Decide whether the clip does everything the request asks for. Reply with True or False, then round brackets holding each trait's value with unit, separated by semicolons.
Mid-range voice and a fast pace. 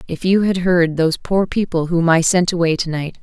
True (175 Hz; 225 wpm)